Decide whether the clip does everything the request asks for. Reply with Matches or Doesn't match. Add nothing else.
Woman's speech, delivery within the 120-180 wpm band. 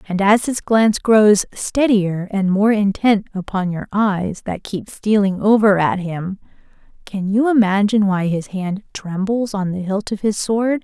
Matches